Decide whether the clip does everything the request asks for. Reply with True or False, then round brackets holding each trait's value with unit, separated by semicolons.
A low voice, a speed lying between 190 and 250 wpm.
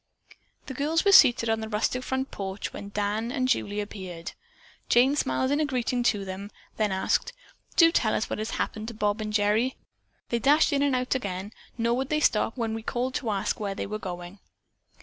False (225 Hz; 205 wpm)